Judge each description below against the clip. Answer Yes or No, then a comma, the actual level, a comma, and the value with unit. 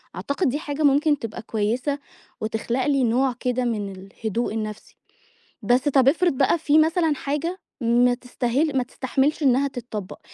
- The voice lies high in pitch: Yes, very high, 255 Hz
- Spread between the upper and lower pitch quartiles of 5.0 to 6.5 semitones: No, average, 3.7 semitones